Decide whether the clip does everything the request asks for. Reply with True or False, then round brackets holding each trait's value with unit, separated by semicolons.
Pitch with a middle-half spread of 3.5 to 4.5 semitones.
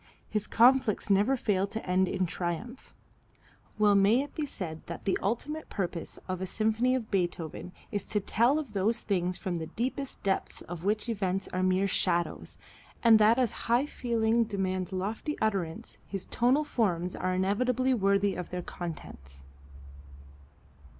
True (4.1 semitones)